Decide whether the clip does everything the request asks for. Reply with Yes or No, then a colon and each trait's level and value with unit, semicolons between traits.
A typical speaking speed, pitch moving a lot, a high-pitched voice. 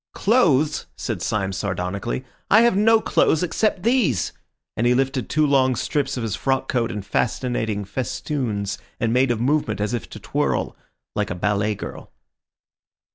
No: average, 160 wpm; wide, 6.3 semitones; low, 125 Hz